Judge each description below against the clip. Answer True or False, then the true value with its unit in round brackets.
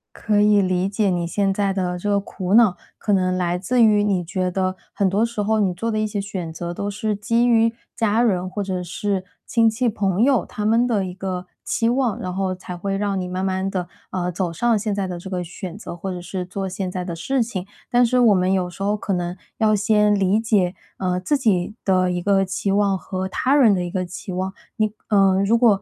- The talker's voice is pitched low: False (195 Hz)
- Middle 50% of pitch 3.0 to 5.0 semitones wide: False (2.6 semitones)